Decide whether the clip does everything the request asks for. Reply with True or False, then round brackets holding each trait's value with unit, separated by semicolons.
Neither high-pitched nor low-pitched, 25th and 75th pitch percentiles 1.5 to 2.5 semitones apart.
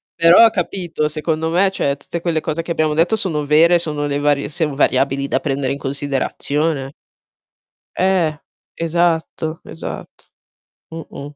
False (155 Hz; 2.9 semitones)